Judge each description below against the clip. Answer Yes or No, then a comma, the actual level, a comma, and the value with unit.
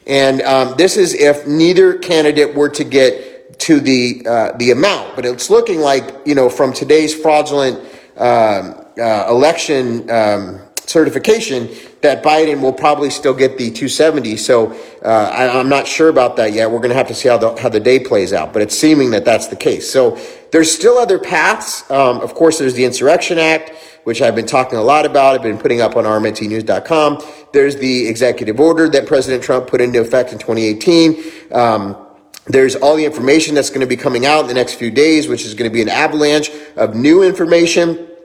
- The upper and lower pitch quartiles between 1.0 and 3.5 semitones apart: No, average, 4.1 semitones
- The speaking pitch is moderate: Yes, medium, 145 Hz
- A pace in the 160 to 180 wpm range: No, average, 200 wpm